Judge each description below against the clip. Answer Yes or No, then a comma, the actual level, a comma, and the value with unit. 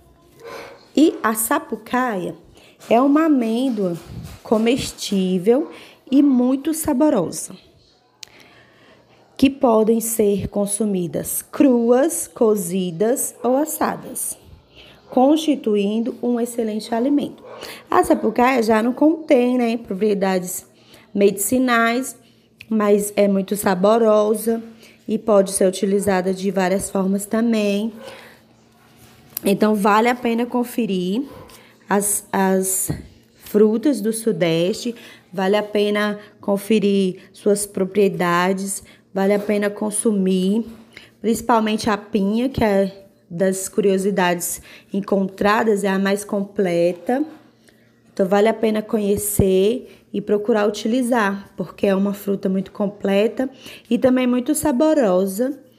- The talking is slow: Yes, slow, 100 wpm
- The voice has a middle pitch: No, high, 215 Hz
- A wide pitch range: No, average, 3.6 semitones